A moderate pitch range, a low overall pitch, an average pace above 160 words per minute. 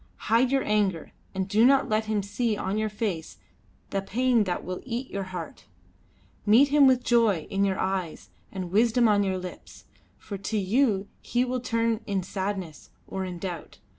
No: average, 3.6 semitones; high, 205 Hz; average, 180 wpm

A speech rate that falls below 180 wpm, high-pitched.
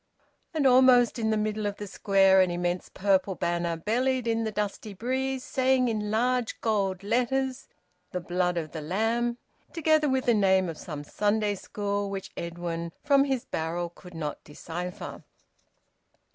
Yes: average, 160 wpm; high, 205 Hz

